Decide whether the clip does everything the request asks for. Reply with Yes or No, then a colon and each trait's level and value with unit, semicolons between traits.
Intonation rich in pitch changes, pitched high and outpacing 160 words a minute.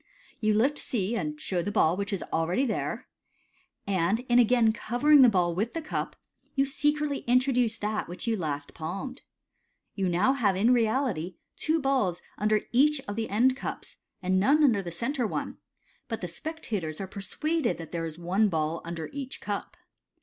Yes: wide, 6.4 semitones; high, 215 Hz; average, 185 wpm